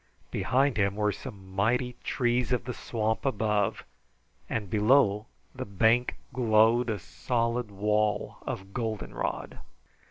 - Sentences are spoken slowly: Yes, slow, 120 wpm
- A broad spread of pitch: No, average, 2.8 semitones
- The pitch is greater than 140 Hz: No, low, 110 Hz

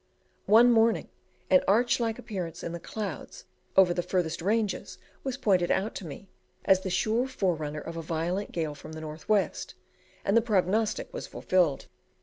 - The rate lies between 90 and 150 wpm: No, average, 170 wpm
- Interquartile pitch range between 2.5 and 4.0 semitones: No, average, 4.8 semitones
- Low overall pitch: No, high, 190 Hz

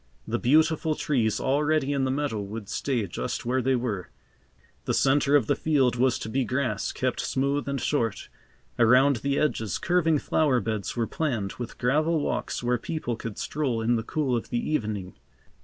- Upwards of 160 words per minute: Yes, average, 180 wpm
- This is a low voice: Yes, low, 130 Hz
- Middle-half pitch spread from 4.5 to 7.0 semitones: No, average, 4.0 semitones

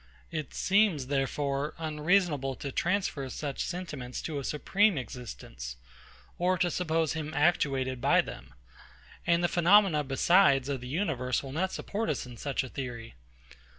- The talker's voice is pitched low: No, medium, 150 Hz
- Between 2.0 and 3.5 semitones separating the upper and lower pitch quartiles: No, average, 4.8 semitones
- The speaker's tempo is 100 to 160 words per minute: Yes, average, 150 wpm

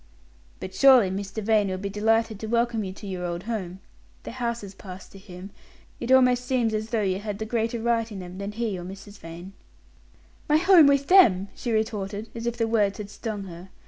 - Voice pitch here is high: Yes, high, 215 Hz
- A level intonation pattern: No, average, 3.3 semitones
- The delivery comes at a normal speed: No, fast, 210 wpm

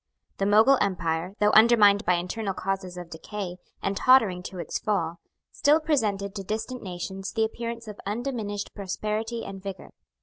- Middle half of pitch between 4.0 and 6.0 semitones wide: No, average, 3.0 semitones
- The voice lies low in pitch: No, high, 205 Hz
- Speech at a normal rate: Yes, average, 160 wpm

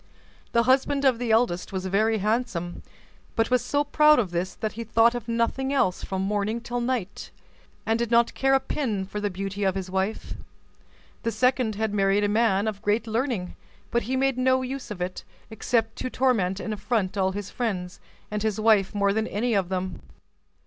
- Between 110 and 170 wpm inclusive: No, average, 195 wpm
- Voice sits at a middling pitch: No, high, 220 Hz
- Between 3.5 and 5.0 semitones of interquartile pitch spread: Yes, average, 3.8 semitones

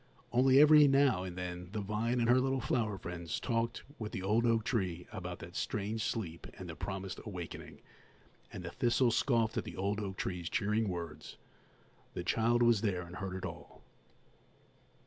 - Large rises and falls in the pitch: No, average, 4.6 semitones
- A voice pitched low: Yes, low, 105 Hz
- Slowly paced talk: No, average, 180 wpm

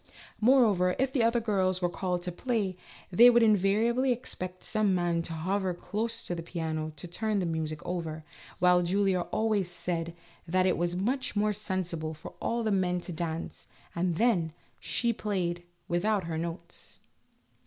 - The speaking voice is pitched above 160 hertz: Yes, medium, 185 Hz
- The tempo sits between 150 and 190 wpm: Yes, average, 175 wpm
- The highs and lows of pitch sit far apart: No, average, 3.9 semitones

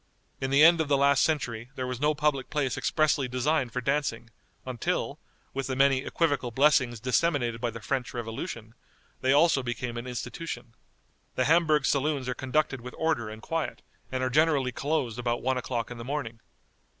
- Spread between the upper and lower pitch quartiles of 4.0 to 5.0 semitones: No, average, 3.5 semitones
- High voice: No, low, 130 Hz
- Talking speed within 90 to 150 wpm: No, average, 180 wpm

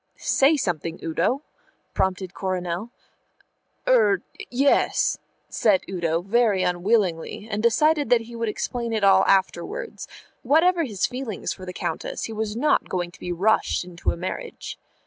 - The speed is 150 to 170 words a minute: No, average, 140 wpm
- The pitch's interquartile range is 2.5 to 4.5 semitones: No, average, 5.1 semitones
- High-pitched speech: Yes, high, 210 Hz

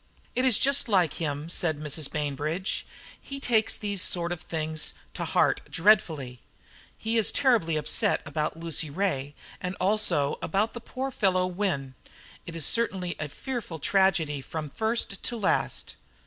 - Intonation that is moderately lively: No, wide, 5.8 semitones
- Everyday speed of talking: Yes, average, 150 wpm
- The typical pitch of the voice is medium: Yes, medium, 175 Hz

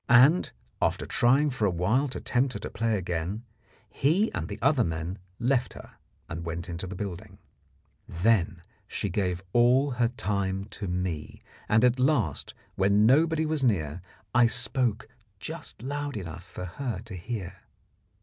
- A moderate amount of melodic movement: No, wide, 6.0 semitones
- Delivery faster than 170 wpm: No, average, 155 wpm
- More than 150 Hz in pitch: No, low, 110 Hz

